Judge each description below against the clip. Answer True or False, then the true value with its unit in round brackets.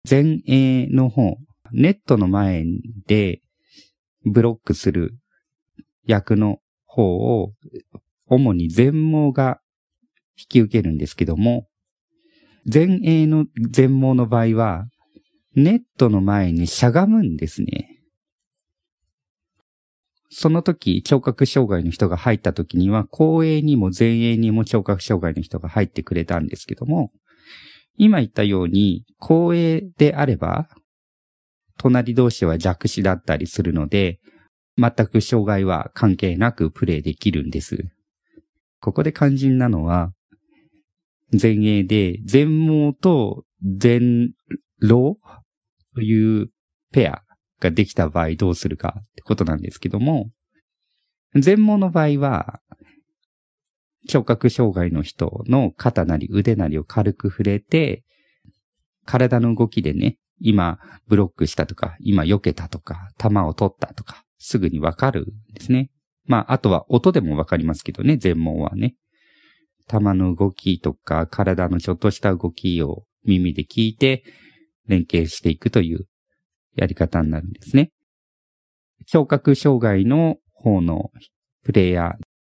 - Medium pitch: False (110 Hz)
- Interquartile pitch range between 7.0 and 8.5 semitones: False (6.3 semitones)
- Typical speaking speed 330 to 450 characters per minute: False (235 characters per minute)